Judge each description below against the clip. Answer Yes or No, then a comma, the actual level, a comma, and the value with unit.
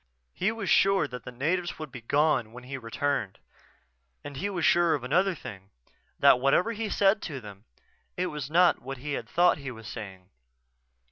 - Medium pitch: Yes, medium, 145 Hz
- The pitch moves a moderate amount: No, wide, 6.2 semitones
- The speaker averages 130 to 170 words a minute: No, average, 195 wpm